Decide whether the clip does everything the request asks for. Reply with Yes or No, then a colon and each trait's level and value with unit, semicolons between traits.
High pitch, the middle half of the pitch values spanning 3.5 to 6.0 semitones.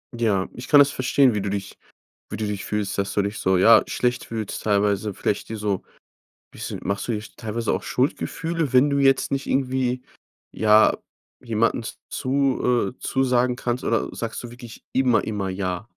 No: low, 115 Hz; average, 3.8 semitones